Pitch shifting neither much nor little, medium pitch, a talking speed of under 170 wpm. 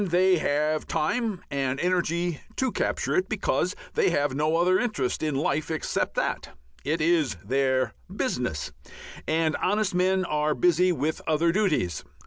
Yes: average, 3.9 semitones; medium, 160 Hz; average, 145 wpm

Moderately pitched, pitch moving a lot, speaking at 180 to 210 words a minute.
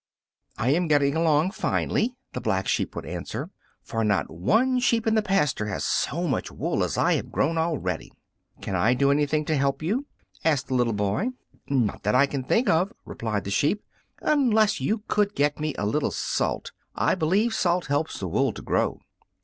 Yes: medium, 150 Hz; wide, 8.1 semitones; average, 190 wpm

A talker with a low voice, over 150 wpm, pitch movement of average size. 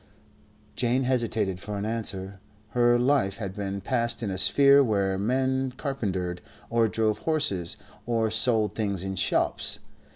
No: low, 110 Hz; average, 140 wpm; average, 4.3 semitones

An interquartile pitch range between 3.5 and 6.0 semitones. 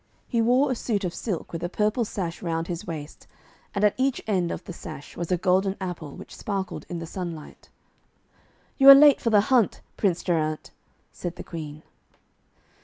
Yes: average, 4.2 semitones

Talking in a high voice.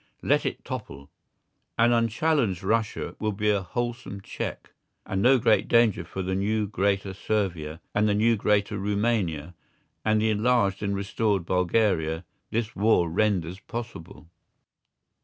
No: low, 105 Hz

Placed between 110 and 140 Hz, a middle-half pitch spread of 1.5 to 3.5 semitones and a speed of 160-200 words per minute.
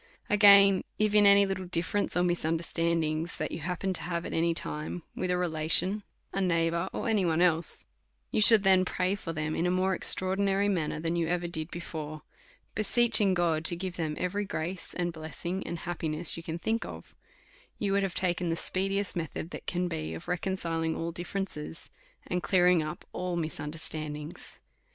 No: medium, 175 Hz; average, 2.7 semitones; average, 180 wpm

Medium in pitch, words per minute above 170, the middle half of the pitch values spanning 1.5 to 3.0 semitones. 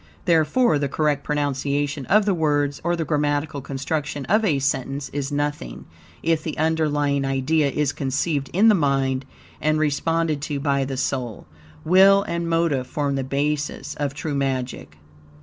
No: medium, 145 Hz; average, 155 wpm; narrow, 2.5 semitones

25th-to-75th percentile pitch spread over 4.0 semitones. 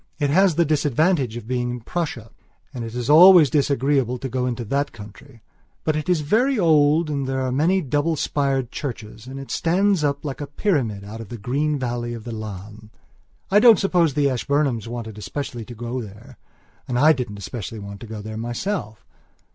Yes: average, 4.7 semitones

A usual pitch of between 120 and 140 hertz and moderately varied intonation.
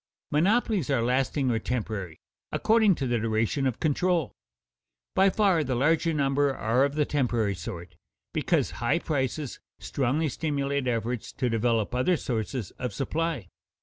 Yes: low, 135 Hz; average, 4.8 semitones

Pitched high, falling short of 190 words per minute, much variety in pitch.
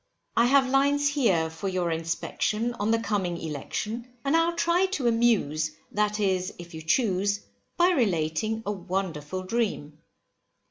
Yes: high, 205 Hz; average, 145 wpm; wide, 5.9 semitones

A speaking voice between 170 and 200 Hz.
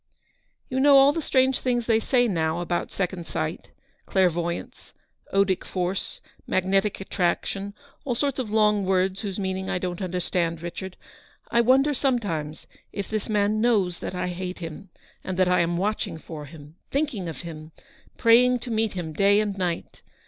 Yes: high, 190 Hz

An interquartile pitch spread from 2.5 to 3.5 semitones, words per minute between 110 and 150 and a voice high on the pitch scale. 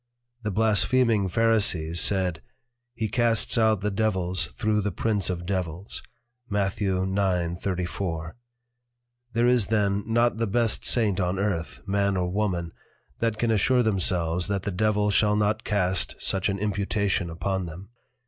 No: average, 2.9 semitones; average, 140 wpm; low, 100 Hz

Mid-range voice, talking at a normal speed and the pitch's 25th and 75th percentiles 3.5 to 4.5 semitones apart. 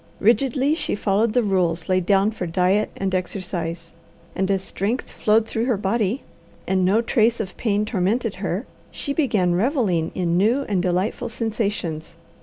No: high, 200 Hz; average, 160 wpm; average, 3.8 semitones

